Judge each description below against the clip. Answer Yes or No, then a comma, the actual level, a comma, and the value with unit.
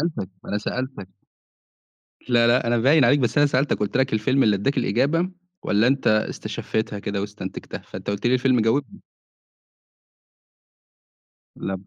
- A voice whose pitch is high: No, low, 120 Hz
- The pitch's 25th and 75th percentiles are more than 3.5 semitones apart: Yes, average, 4.2 semitones